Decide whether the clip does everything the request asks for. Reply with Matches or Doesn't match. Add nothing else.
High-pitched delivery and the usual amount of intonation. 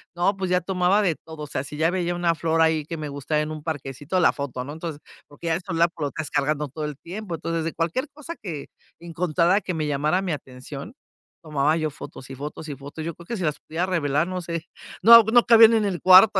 Doesn't match